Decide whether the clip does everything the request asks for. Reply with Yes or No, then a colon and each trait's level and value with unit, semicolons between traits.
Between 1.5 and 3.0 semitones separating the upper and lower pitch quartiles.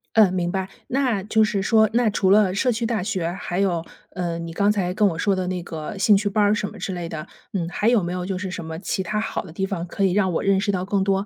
Yes: narrow, 2.6 semitones